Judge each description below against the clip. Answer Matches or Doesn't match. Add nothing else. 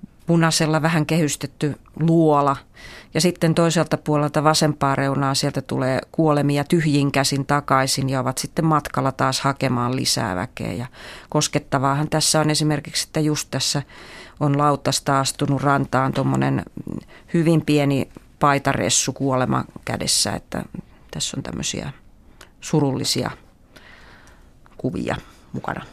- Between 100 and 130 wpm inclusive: Matches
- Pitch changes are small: Matches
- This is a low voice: Doesn't match